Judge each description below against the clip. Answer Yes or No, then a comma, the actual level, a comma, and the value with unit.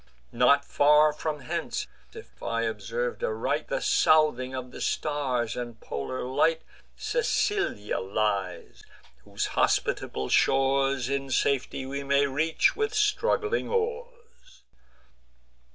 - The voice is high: No, medium, 140 Hz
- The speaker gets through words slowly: Yes, slow, 110 wpm